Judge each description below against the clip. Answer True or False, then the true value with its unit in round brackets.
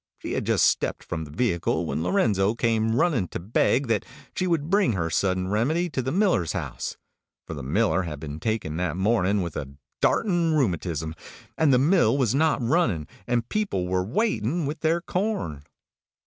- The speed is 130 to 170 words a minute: False (180 wpm)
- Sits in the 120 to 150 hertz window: False (110 Hz)